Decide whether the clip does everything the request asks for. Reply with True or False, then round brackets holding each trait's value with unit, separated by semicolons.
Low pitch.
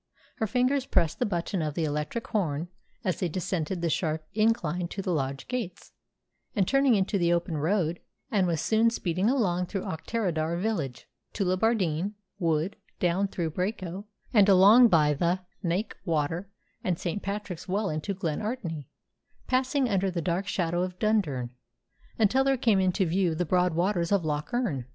False (185 Hz)